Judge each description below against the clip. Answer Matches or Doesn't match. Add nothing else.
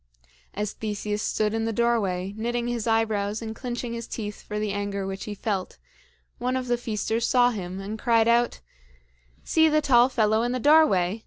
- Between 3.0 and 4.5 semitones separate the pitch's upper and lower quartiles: Doesn't match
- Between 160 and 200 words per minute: Matches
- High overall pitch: Matches